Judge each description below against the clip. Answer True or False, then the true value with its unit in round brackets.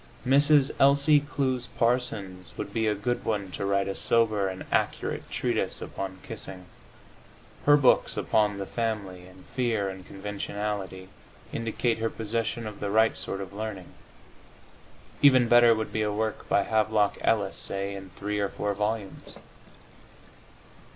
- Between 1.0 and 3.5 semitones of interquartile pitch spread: True (2.9 semitones)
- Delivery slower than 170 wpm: True (145 wpm)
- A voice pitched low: True (105 Hz)